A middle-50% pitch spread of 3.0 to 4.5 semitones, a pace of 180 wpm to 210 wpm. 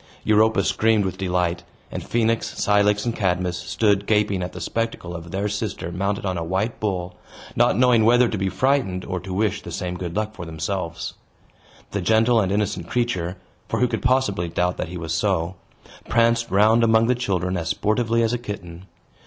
Yes: average, 3.9 semitones; average, 190 wpm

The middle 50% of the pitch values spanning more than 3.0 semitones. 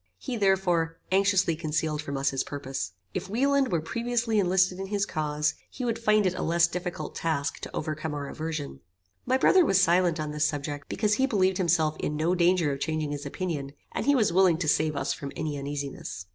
Yes: average, 4.3 semitones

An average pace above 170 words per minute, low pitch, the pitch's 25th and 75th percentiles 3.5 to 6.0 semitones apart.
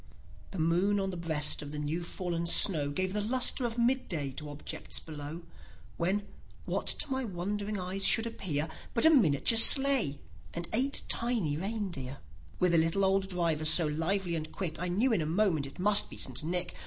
No: average, 190 wpm; medium, 180 Hz; average, 4.8 semitones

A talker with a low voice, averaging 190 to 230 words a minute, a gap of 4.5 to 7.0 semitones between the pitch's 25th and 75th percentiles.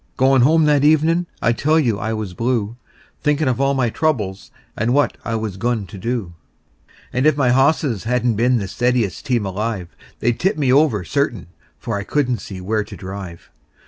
Yes: low, 120 Hz; average, 195 wpm; average, 5.1 semitones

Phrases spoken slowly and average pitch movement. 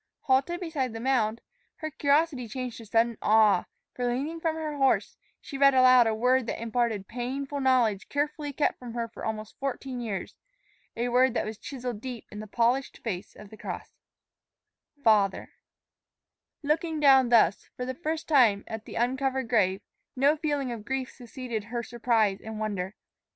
No: average, 170 wpm; average, 3.6 semitones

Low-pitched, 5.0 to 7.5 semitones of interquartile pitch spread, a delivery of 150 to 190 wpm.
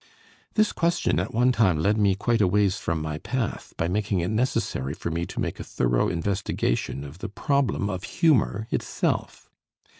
Yes: low, 100 Hz; wide, 5.4 semitones; average, 180 wpm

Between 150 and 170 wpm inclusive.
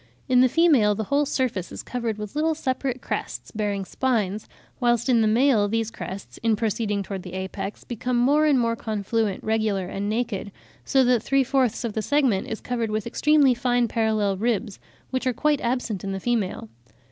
No: average, 190 wpm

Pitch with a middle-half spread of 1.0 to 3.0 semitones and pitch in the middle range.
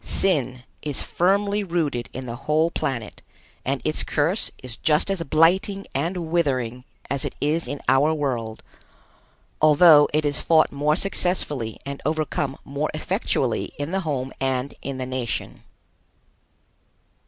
No: average, 4.0 semitones; medium, 145 Hz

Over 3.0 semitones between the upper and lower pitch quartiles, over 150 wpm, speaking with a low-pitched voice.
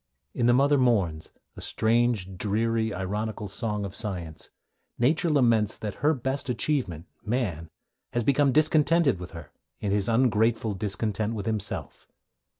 No: average, 4.1 semitones; average, 140 wpm; low, 110 Hz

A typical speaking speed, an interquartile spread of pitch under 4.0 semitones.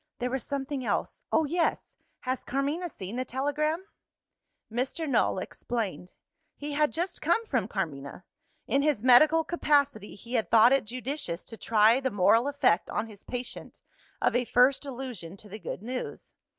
No: average, 165 wpm; average, 4.8 semitones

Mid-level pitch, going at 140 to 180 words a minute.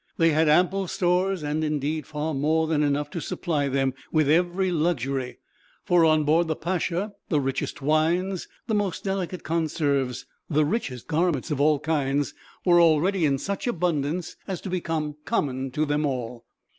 Yes: medium, 155 Hz; average, 165 wpm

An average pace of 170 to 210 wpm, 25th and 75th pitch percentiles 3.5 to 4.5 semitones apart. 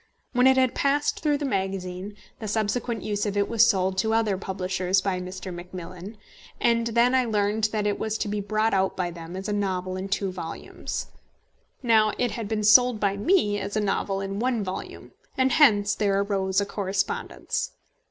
No: average, 190 wpm; average, 2.8 semitones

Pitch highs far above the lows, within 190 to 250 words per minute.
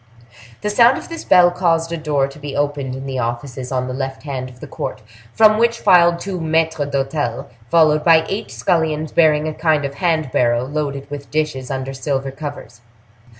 No: average, 3.5 semitones; average, 195 wpm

